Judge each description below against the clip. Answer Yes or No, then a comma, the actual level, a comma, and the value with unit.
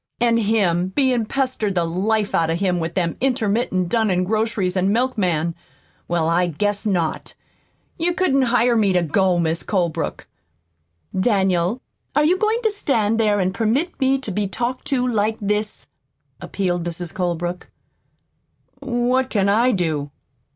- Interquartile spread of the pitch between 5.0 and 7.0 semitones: Yes, average, 5.3 semitones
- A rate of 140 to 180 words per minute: Yes, average, 150 wpm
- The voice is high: Yes, high, 205 Hz